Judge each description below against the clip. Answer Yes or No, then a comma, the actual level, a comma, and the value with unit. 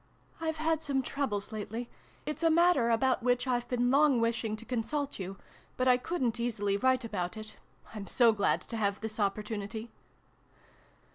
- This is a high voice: Yes, high, 235 Hz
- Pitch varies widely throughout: No, average, 3.4 semitones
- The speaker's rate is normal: Yes, average, 170 wpm